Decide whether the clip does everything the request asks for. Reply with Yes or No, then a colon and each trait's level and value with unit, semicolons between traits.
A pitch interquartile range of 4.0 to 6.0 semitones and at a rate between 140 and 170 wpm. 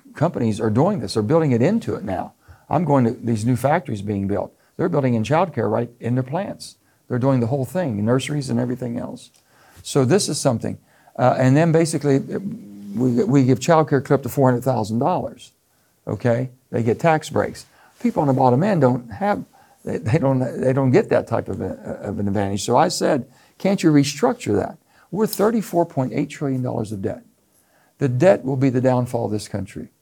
No: average, 4.6 semitones; average, 190 wpm